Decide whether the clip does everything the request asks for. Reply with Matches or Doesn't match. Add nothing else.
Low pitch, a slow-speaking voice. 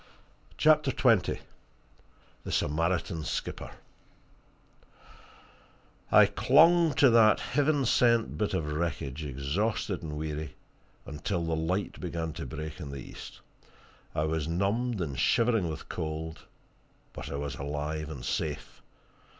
Matches